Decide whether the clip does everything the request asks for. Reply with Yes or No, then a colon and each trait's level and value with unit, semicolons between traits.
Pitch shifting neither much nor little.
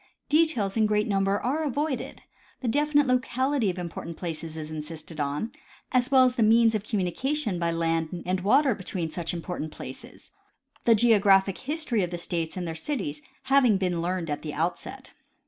No: wide, 7.1 semitones